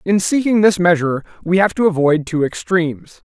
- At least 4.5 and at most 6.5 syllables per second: Yes, 5.5 syllables/s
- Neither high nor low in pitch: Yes, medium, 175 Hz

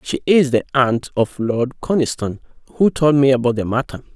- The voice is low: Yes, low, 130 Hz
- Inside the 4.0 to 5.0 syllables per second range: No, 5.2 syllables/s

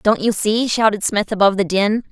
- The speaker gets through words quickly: Yes, fast, 225 wpm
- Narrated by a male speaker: No, female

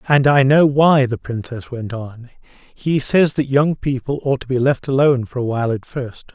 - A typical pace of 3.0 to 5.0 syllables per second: Yes, 4.8 syllables/s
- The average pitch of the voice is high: No, low, 130 Hz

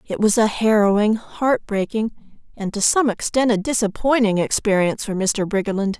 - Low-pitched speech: No, high, 210 Hz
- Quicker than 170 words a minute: No, average, 160 wpm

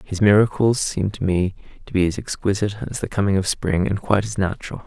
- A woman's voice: No, male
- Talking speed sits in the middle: No, fast, 220 wpm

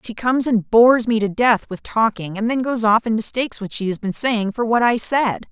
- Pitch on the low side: No, high, 225 Hz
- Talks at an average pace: No, fast, 260 wpm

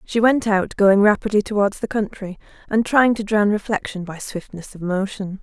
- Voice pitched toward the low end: No, high, 205 Hz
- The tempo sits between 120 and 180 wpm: No, average, 190 wpm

